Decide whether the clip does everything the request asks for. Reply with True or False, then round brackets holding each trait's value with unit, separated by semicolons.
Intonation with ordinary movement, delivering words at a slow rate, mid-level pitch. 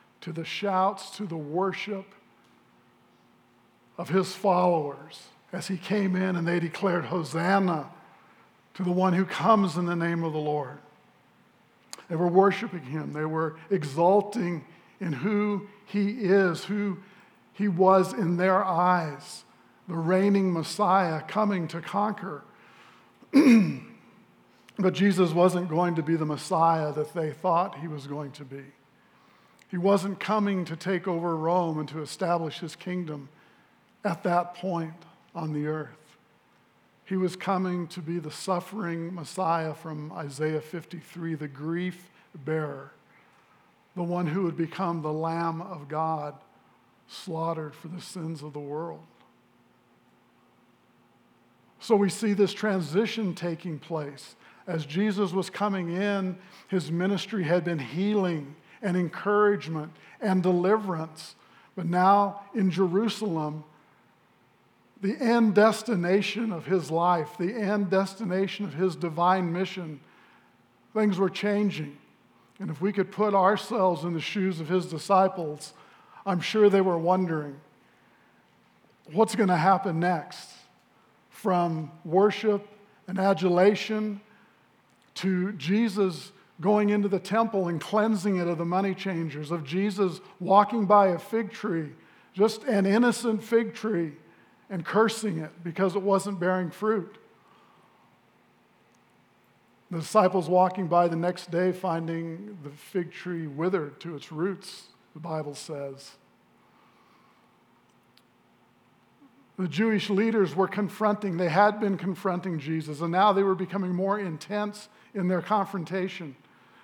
True (3.4 semitones; 130 wpm; 180 Hz)